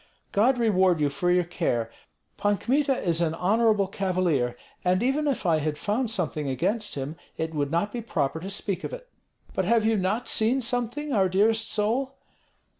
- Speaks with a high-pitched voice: Yes, high, 200 Hz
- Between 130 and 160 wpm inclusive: No, average, 185 wpm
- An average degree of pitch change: No, wide, 5.7 semitones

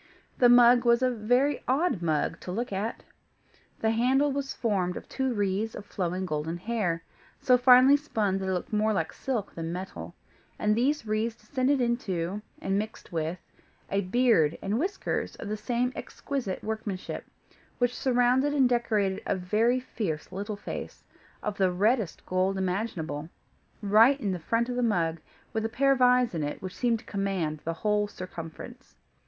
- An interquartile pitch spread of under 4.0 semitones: No, average, 4.9 semitones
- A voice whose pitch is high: Yes, high, 215 Hz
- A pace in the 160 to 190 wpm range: Yes, average, 170 wpm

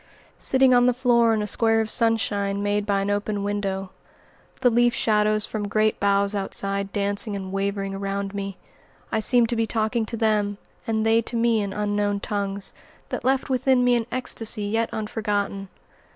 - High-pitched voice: Yes, high, 210 Hz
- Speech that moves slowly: No, average, 180 wpm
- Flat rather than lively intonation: Yes, narrow, 2.2 semitones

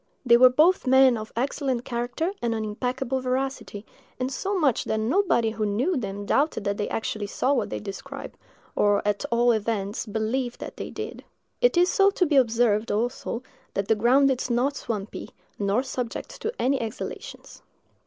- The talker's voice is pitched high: Yes, high, 240 Hz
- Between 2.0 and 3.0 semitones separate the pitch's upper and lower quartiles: No, average, 3.6 semitones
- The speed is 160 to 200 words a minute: Yes, average, 165 wpm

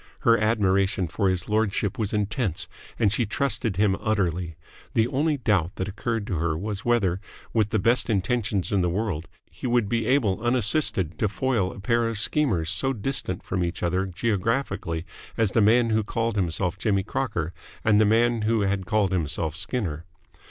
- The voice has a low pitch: Yes, low, 105 Hz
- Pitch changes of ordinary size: Yes, average, 3.7 semitones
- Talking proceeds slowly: No, average, 180 wpm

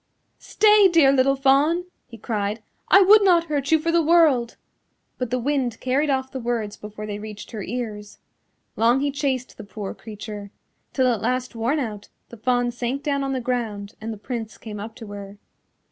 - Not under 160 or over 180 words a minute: No, average, 190 wpm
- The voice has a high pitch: Yes, high, 245 Hz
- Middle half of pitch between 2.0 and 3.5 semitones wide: No, average, 4.4 semitones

